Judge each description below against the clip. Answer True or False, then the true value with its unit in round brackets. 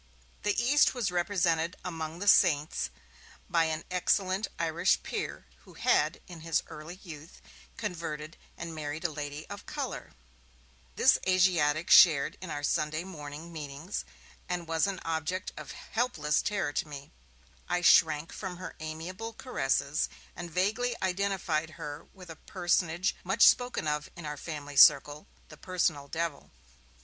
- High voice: False (165 Hz)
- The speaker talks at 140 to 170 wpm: True (145 wpm)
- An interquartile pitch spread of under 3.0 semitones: False (3.3 semitones)